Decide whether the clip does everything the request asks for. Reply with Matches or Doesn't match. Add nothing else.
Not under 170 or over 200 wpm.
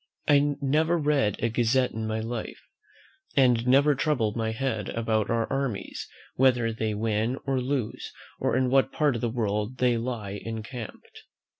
Doesn't match